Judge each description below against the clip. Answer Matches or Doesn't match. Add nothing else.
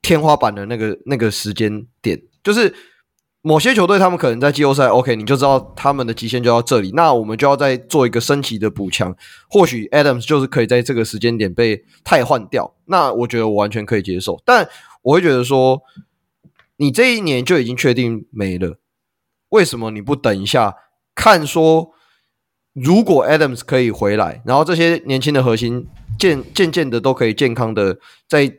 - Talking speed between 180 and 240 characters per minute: Doesn't match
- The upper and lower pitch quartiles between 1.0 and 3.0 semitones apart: Doesn't match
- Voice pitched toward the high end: Doesn't match